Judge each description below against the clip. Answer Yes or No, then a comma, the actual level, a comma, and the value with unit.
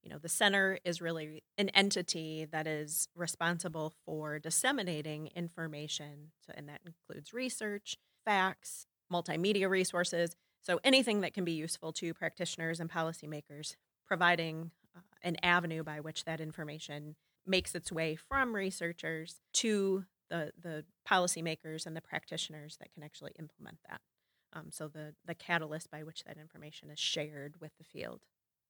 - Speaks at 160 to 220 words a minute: No, average, 150 wpm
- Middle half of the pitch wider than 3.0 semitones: No, narrow, 2.5 semitones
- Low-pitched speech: No, medium, 165 Hz